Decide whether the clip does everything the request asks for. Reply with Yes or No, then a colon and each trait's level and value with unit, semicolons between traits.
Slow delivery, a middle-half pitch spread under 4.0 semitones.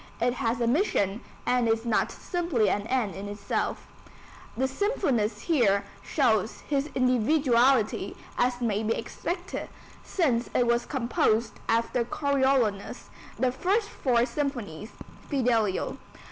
Yes: slow, 120 wpm; average, 3.6 semitones